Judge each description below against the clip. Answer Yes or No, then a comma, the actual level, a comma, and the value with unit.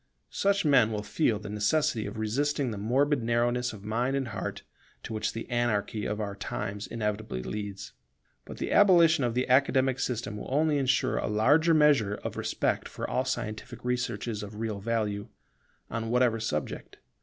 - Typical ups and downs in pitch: Yes, average, 4.0 semitones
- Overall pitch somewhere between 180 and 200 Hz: No, low, 115 Hz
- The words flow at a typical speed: Yes, average, 170 wpm